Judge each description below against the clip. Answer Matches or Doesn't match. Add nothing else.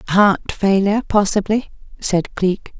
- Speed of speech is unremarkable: Doesn't match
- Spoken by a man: Doesn't match